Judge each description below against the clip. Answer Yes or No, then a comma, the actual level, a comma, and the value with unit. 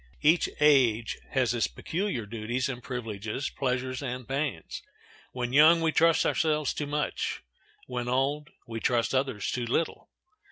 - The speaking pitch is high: No, low, 130 Hz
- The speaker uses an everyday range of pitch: Yes, average, 3.7 semitones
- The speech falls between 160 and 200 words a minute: No, average, 145 wpm